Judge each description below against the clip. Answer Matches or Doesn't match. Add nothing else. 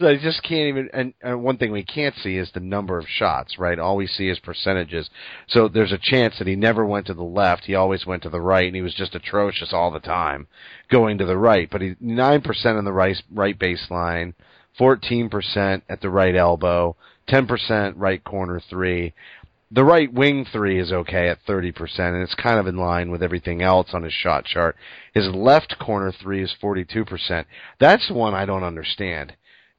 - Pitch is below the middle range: Matches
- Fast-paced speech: Matches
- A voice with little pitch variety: Doesn't match